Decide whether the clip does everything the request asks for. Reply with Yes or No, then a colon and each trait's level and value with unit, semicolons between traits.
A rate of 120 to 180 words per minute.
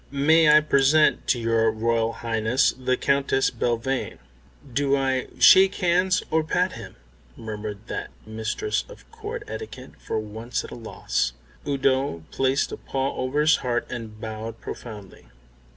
Yes: average, 145 wpm